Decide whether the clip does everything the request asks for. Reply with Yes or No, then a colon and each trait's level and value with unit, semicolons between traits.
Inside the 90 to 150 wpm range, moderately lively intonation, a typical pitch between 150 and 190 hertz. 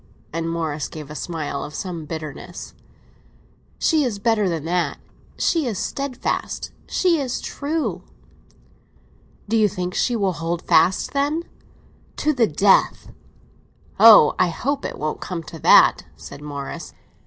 No: slow, 135 wpm; wide, 7.3 semitones; medium, 185 Hz